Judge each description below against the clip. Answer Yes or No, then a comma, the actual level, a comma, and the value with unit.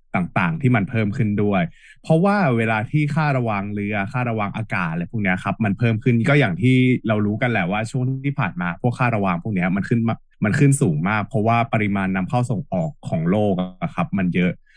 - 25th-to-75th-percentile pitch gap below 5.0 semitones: No, average, 5.3 semitones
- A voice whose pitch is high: No, low, 115 Hz